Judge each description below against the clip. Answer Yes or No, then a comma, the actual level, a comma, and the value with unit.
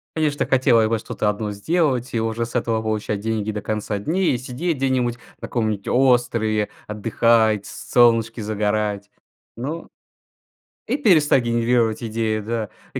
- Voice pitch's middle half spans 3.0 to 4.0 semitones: No, narrow, 2.6 semitones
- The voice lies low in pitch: Yes, low, 115 Hz